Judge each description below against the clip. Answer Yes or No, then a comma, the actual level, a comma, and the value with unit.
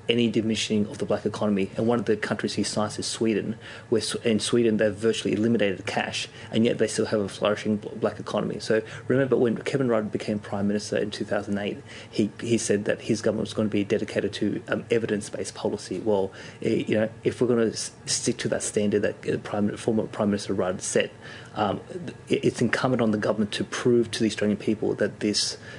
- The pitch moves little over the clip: Yes, narrow, 1.8 semitones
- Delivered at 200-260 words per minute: Yes, fast, 205 wpm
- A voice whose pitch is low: Yes, low, 110 Hz